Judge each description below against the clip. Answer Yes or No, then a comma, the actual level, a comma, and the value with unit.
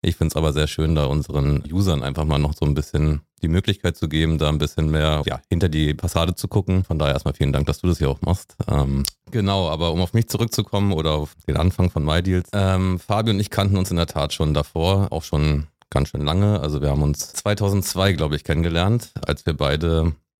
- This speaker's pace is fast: Yes, fast, 235 wpm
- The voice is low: Yes, very low, 80 Hz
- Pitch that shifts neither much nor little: Yes, average, 4.0 semitones